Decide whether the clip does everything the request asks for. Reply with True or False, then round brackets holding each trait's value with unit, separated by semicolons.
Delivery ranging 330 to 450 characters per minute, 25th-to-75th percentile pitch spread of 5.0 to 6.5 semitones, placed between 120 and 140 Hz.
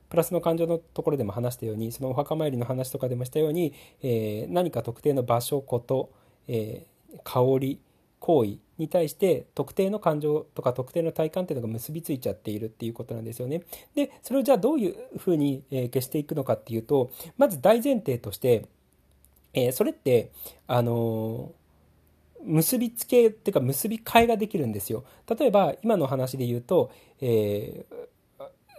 True (350 characters per minute; 6.2 semitones; 135 Hz)